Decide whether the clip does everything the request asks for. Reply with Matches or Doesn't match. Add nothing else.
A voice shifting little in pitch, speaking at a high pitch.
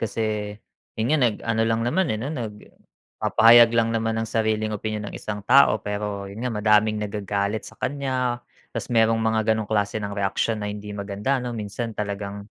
Doesn't match